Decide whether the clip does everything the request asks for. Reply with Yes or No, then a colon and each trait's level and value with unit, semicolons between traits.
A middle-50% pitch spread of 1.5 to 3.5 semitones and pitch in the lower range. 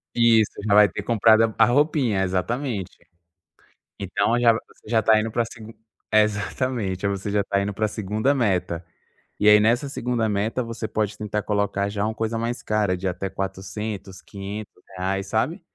Yes: narrow, 2.4 semitones; low, 105 Hz